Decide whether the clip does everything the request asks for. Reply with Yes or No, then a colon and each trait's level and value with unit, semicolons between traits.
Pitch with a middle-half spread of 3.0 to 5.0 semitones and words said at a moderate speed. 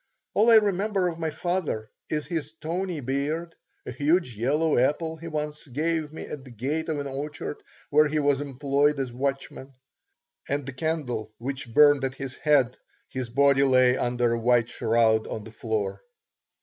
Yes: average, 3.9 semitones; average, 175 wpm